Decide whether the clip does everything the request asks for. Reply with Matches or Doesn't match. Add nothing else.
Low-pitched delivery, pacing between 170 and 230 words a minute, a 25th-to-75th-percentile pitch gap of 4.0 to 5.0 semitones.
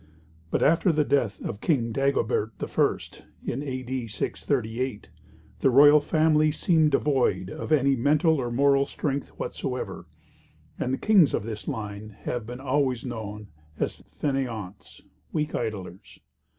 Doesn't match